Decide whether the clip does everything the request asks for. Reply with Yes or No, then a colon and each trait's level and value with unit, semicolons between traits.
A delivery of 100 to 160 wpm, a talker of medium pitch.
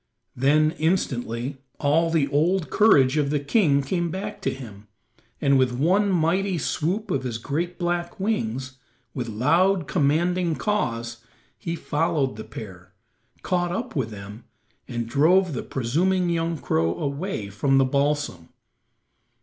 Yes: average, 140 wpm; medium, 145 Hz